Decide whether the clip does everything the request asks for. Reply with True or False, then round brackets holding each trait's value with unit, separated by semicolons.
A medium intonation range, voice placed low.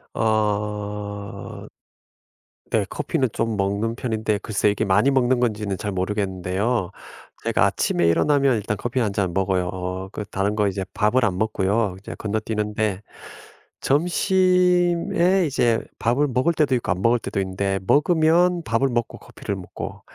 True (4.6 semitones; 110 Hz)